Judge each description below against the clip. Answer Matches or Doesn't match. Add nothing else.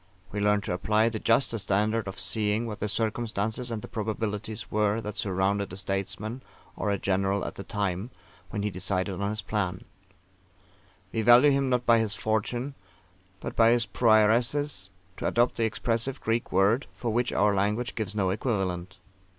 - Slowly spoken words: Doesn't match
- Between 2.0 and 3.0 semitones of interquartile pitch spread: Matches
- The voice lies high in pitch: Doesn't match